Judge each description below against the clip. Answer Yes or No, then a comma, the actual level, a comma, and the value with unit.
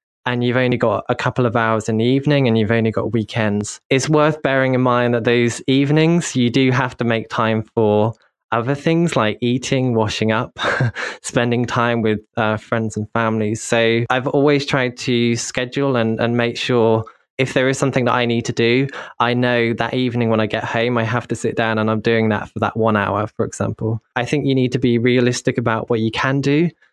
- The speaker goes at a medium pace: No, fast, 220 wpm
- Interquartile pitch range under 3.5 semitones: Yes, narrow, 2.5 semitones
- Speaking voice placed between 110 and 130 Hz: Yes, low, 120 Hz